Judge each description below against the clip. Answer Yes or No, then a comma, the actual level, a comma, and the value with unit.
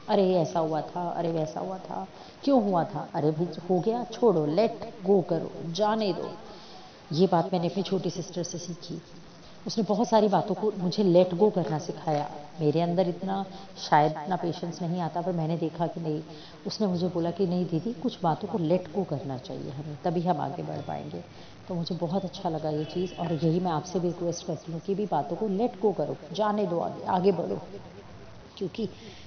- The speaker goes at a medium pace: No, fast, 200 wpm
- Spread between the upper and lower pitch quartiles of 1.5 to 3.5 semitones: Yes, average, 2.9 semitones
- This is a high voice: No, medium, 175 Hz